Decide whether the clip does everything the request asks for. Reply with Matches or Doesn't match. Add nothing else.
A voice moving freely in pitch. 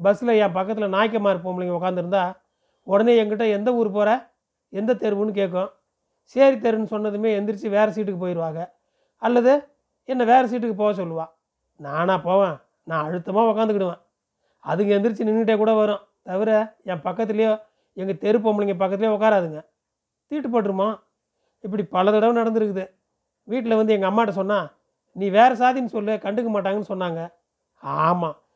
Doesn't match